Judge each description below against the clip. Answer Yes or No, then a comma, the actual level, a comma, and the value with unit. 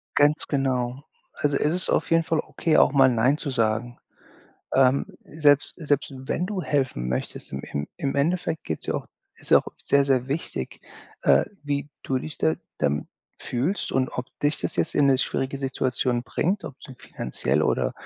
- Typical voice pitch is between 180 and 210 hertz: No, low, 135 Hz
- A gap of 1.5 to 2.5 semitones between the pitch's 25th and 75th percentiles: No, average, 2.9 semitones